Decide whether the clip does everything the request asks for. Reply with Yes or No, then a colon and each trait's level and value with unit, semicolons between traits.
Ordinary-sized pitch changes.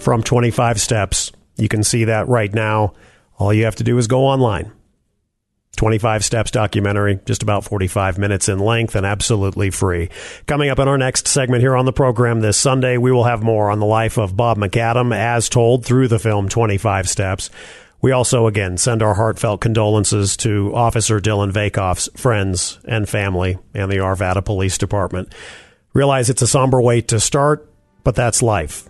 Yes: average, 3.1 semitones